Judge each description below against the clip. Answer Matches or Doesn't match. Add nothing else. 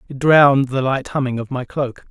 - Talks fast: Matches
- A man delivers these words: Matches